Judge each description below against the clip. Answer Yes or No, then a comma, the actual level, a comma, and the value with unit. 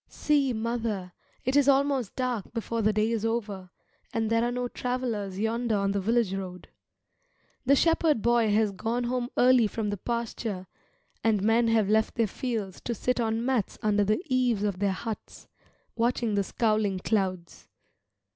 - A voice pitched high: Yes, high, 225 Hz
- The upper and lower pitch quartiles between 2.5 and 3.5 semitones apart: Yes, average, 3.0 semitones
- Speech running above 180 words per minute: No, average, 165 wpm